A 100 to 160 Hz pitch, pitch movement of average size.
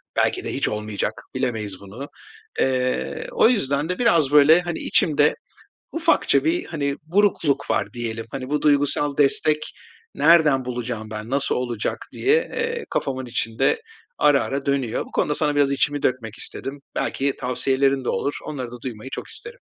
Yes: medium, 140 Hz; average, 3.4 semitones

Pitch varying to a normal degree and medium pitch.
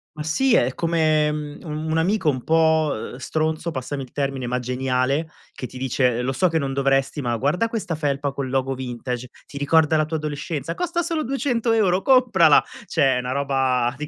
Yes: average, 3.7 semitones; medium, 145 Hz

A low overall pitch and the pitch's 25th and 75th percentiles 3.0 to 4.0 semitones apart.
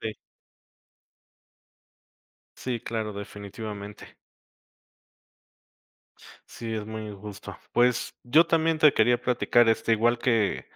No: low, 115 Hz; narrow, 2.4 semitones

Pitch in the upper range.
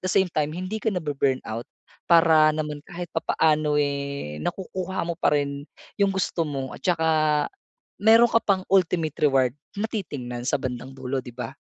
No: medium, 155 Hz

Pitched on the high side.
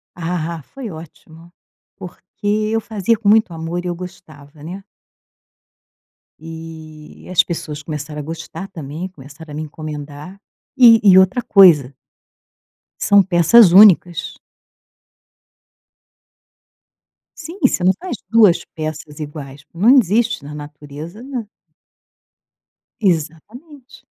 No: medium, 170 Hz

